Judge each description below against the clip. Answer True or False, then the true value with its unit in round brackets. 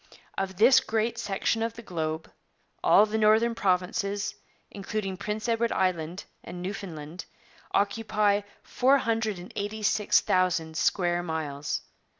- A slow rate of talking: True (110 wpm)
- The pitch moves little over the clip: False (3.5 semitones)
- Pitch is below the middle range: False (200 Hz)